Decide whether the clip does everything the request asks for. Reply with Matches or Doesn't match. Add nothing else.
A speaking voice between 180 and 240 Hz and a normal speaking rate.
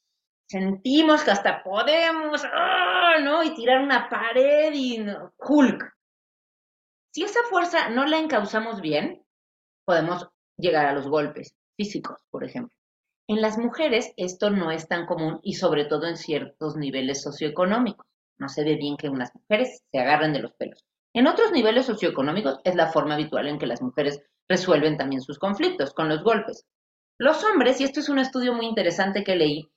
Matches